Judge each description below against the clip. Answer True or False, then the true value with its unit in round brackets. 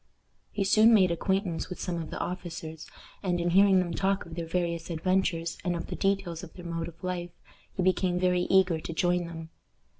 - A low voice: False (175 Hz)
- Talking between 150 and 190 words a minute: False (205 wpm)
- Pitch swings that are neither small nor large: False (1.9 semitones)